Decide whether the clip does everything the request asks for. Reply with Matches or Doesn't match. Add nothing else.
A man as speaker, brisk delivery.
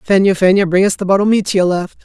Matches